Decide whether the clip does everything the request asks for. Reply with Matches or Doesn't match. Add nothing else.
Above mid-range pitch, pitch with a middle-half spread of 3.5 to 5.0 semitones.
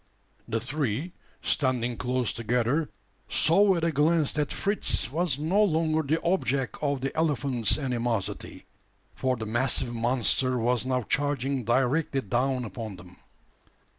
Doesn't match